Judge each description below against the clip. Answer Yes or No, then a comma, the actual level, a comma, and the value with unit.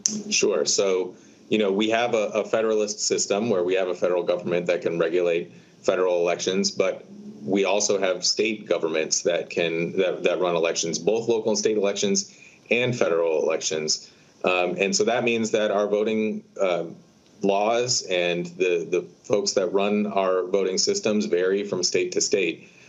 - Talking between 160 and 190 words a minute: Yes, average, 170 wpm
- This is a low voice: Yes, low, 125 Hz